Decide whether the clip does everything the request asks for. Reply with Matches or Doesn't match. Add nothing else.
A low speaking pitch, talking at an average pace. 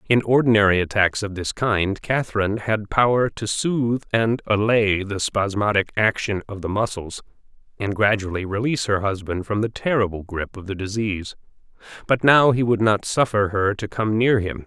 Matches